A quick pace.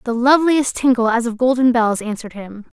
No: average, 195 wpm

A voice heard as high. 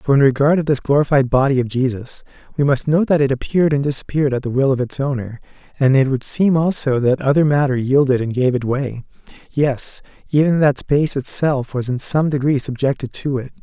No: low, 135 Hz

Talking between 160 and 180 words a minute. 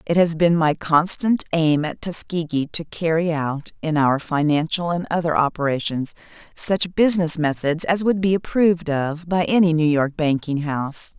Yes: average, 165 wpm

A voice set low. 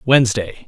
Yes: low, 120 Hz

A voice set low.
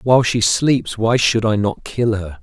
Yes: low, 110 Hz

